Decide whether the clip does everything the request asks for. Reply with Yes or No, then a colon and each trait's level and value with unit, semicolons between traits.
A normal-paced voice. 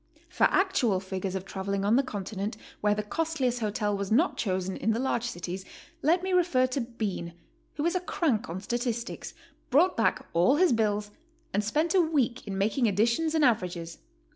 Yes: average, 185 wpm